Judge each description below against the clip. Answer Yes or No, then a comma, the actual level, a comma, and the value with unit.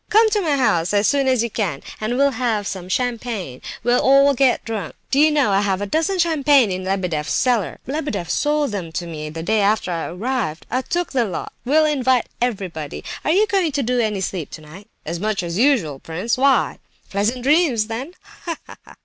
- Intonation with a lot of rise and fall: Yes, wide, 6.8 semitones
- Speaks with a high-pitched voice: Yes, high, 230 Hz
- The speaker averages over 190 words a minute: Yes, average, 200 wpm